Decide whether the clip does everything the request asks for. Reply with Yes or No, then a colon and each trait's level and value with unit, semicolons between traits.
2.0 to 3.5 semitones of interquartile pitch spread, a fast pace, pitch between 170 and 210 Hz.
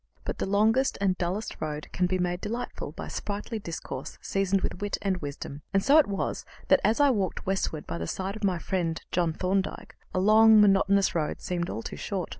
Yes: average, 3.0 semitones; fast, 210 wpm; high, 190 Hz